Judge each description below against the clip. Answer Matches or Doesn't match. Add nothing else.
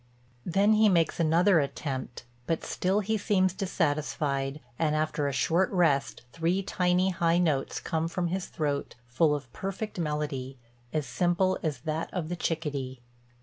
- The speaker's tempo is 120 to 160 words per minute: Matches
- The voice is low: Doesn't match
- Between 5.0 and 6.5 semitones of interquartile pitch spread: Doesn't match